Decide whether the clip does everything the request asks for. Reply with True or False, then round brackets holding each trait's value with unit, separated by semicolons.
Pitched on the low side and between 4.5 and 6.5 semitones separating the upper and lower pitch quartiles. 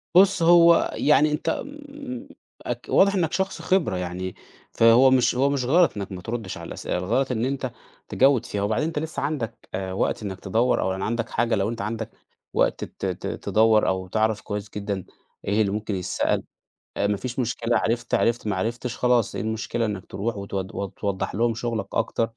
True (115 Hz; 4.8 semitones)